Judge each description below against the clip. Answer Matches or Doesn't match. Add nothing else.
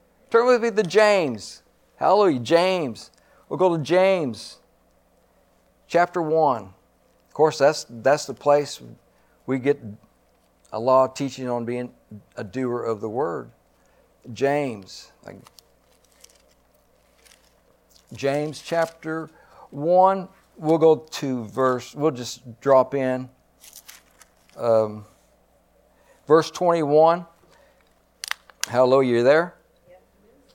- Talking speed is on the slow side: Matches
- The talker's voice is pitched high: Doesn't match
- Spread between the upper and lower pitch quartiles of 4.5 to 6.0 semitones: Matches